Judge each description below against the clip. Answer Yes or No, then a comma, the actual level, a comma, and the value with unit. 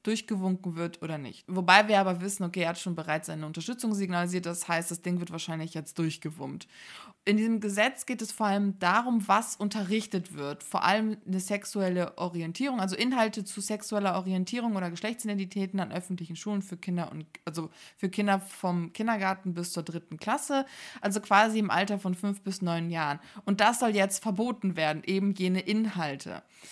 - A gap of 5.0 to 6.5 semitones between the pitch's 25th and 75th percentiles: No, average, 3.6 semitones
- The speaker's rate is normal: Yes, average, 180 wpm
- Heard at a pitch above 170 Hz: Yes, high, 190 Hz